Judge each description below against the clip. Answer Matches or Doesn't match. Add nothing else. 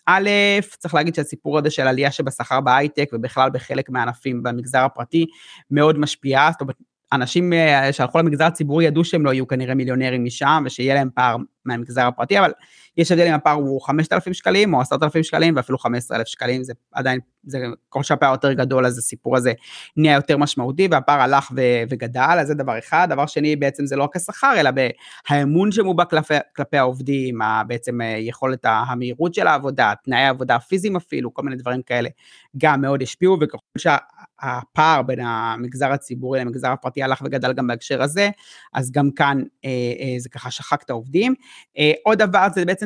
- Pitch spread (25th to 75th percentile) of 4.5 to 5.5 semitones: Doesn't match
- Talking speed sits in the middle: Doesn't match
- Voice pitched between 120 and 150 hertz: Matches